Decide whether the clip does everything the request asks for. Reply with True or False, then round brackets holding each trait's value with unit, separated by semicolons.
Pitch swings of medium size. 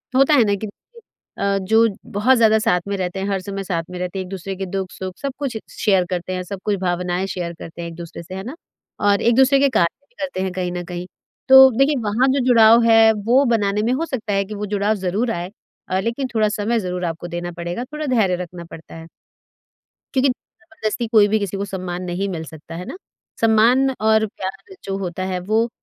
True (4.1 semitones)